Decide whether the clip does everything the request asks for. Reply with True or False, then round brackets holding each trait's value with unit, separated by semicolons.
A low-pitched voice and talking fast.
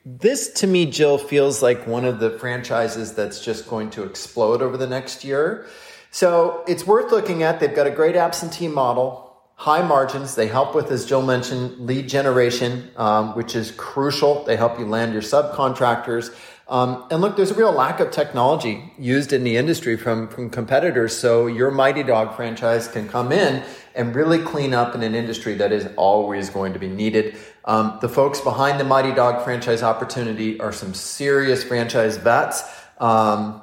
False (125 Hz; 185 wpm)